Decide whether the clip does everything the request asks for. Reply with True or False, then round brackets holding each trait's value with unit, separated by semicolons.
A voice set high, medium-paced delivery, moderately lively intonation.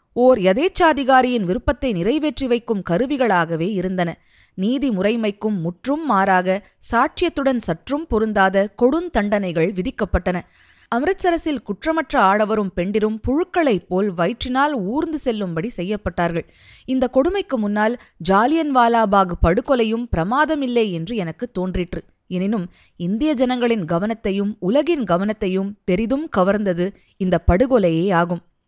False (215 Hz; 95 wpm; 5.8 semitones)